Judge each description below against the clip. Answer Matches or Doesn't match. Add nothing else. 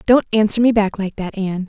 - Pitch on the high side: Matches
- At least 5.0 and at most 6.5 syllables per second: Matches